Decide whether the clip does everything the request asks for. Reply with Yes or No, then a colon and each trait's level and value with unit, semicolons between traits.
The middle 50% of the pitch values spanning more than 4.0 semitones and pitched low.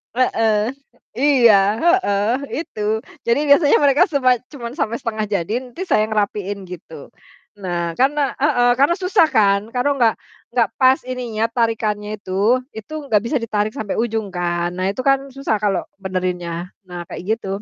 No: average, 4.4 semitones; high, 220 Hz